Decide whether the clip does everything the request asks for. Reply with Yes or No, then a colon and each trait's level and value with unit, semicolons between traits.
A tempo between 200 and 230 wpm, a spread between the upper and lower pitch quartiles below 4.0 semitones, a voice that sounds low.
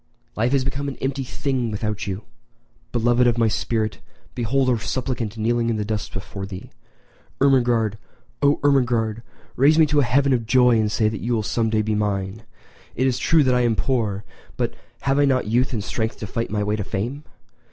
Yes: fast, 205 wpm; average, 3.3 semitones; low, 115 Hz